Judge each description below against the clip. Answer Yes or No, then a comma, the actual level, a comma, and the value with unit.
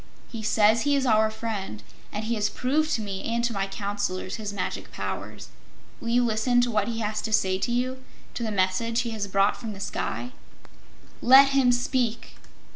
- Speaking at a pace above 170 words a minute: Yes, average, 200 wpm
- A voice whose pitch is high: Yes, high, 220 Hz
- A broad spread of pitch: No, average, 3.0 semitones